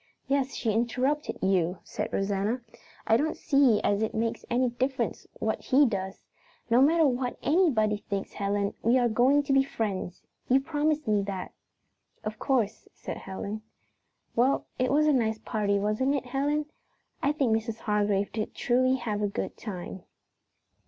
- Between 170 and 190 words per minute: No, average, 160 wpm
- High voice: Yes, high, 235 Hz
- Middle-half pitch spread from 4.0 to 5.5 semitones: Yes, average, 4.7 semitones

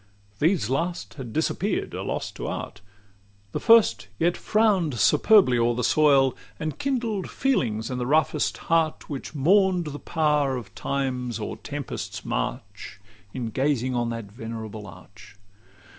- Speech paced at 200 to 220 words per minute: No, average, 145 wpm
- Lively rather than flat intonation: Yes, wide, 6.4 semitones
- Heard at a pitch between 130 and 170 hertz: Yes, low, 135 Hz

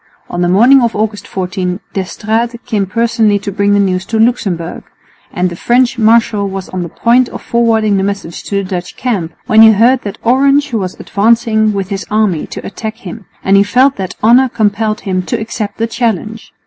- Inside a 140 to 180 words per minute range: No, average, 200 wpm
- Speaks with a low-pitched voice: No, high, 215 Hz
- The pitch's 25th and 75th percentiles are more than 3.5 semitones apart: No, average, 3.2 semitones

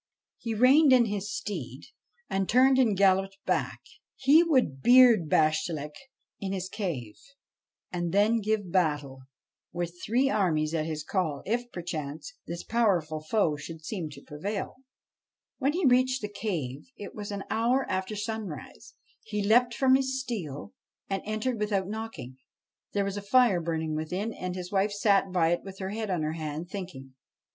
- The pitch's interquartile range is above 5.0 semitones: Yes, wide, 5.6 semitones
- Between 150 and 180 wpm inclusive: Yes, average, 165 wpm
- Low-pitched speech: No, high, 195 Hz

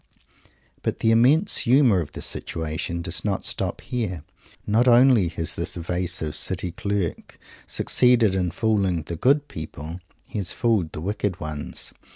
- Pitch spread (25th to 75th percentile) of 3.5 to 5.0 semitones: No, wide, 5.5 semitones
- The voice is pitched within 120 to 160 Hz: No, very low, 95 Hz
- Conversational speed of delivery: Yes, average, 150 wpm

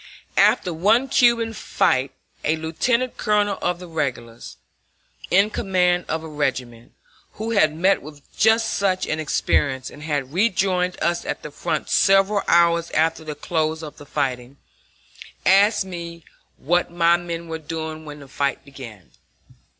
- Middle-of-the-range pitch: Yes, medium, 170 Hz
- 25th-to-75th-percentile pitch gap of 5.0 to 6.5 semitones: No, average, 4.4 semitones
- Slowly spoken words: No, average, 150 wpm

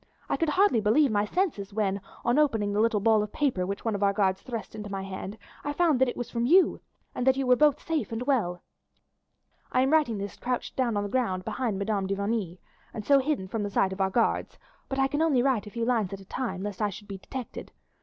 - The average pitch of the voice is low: No, high, 225 Hz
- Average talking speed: No, fast, 255 wpm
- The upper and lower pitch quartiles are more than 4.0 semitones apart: Yes, average, 4.7 semitones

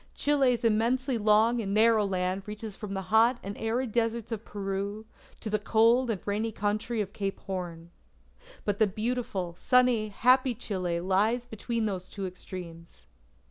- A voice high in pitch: Yes, high, 215 Hz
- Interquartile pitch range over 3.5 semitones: No, average, 3.1 semitones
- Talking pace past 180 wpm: No, average, 155 wpm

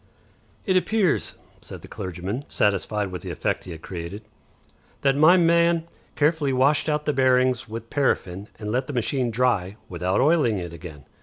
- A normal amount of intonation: No, wide, 7.7 semitones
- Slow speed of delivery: No, average, 165 wpm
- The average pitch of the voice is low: Yes, low, 125 Hz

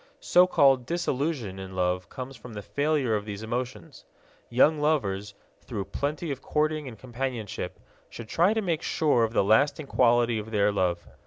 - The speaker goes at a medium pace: Yes, average, 170 wpm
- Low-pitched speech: Yes, low, 125 Hz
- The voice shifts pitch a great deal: Yes, wide, 6.1 semitones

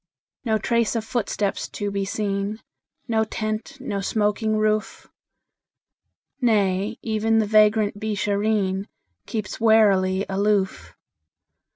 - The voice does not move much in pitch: Yes, narrow, 1.7 semitones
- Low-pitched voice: No, high, 215 Hz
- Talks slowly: Yes, slow, 100 wpm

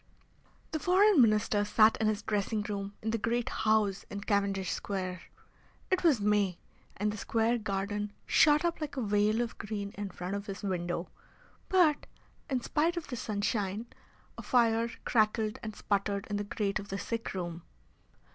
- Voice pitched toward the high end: Yes, high, 210 Hz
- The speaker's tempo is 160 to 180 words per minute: Yes, average, 170 wpm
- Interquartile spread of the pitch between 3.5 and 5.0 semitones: No, narrow, 2.5 semitones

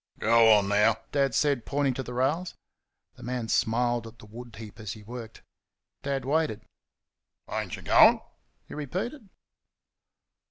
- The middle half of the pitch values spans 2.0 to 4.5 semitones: Yes, average, 4.0 semitones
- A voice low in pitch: Yes, low, 120 Hz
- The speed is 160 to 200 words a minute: No, average, 150 wpm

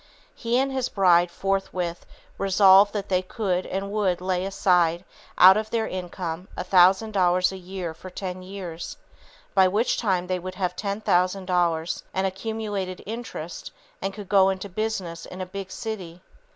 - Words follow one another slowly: No, average, 165 wpm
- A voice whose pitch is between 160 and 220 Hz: Yes, high, 190 Hz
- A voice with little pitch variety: Yes, narrow, 1.8 semitones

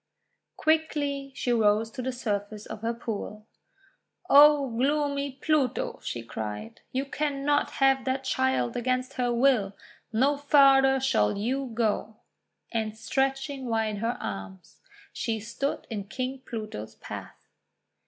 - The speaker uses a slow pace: Yes, slow, 125 wpm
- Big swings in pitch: No, average, 4.3 semitones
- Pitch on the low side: No, very high, 250 Hz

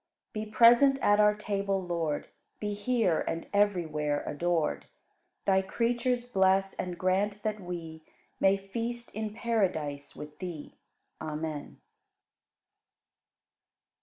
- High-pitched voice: Yes, high, 195 Hz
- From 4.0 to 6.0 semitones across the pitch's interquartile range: Yes, average, 4.4 semitones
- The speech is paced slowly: Yes, slow, 110 wpm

